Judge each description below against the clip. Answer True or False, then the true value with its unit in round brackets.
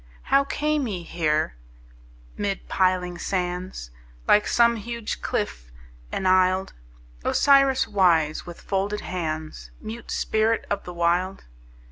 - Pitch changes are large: False (4.1 semitones)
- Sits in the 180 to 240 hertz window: True (185 Hz)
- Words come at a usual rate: False (110 wpm)